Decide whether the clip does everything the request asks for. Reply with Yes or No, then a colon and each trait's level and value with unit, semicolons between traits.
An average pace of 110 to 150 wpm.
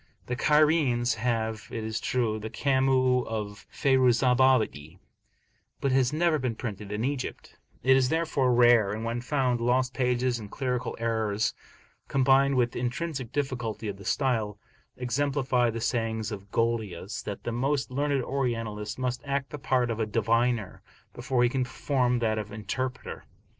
No: average, 160 wpm